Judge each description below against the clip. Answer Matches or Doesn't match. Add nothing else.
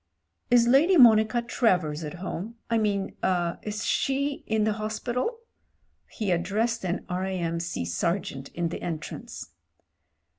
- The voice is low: Doesn't match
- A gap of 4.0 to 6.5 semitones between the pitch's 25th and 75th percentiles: Matches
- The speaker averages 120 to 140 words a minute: Matches